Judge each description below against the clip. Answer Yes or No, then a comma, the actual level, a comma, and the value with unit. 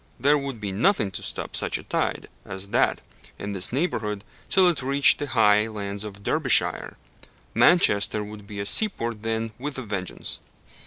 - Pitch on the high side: No, low, 110 Hz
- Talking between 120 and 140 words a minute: No, average, 170 wpm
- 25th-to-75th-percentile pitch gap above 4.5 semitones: Yes, average, 5.3 semitones